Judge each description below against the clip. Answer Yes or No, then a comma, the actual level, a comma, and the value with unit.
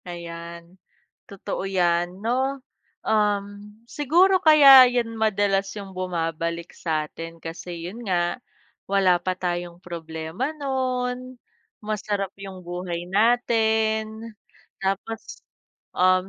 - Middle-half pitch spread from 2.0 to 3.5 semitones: No, average, 4.5 semitones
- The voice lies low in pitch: No, high, 195 Hz